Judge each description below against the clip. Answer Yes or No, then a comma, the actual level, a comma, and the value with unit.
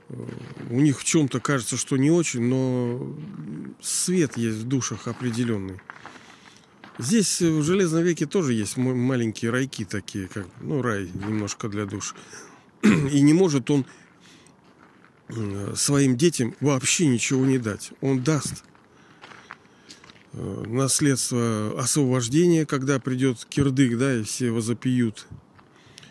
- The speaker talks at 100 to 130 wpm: Yes, average, 115 wpm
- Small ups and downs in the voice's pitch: No, average, 3.8 semitones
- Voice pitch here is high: No, low, 130 Hz